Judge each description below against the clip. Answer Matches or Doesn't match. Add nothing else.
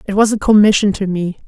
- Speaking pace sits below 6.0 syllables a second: Doesn't match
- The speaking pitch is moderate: Doesn't match